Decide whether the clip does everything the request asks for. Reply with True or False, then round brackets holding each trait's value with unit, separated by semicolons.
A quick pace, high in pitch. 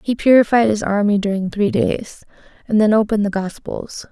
False (175 wpm; 210 Hz)